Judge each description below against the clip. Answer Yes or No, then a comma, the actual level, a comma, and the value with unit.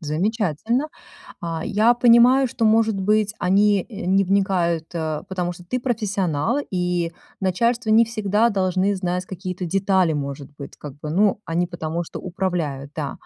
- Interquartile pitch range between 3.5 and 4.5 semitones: Yes, average, 4.1 semitones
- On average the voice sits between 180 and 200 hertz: Yes, high, 190 Hz